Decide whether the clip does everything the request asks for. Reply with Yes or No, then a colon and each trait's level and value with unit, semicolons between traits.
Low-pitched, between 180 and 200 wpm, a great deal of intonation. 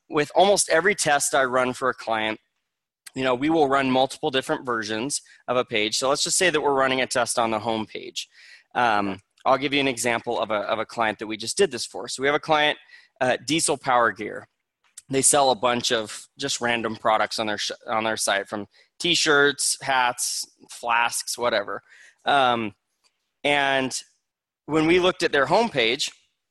No: low, 125 Hz; average, 195 wpm; average, 4.2 semitones